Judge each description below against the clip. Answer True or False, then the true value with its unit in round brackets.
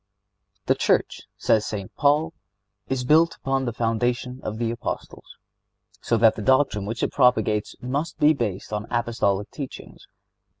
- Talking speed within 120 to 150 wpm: True (145 wpm)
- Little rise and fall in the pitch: False (3.7 semitones)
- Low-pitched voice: True (120 Hz)